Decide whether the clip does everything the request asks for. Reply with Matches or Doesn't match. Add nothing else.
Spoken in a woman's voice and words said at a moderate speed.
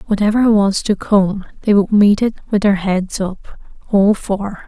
Matches